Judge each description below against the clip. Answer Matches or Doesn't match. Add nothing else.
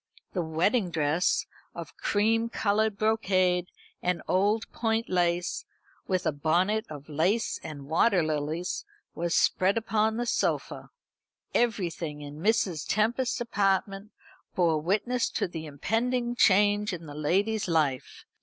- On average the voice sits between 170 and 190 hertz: Matches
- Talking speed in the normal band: Doesn't match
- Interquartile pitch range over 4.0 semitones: Matches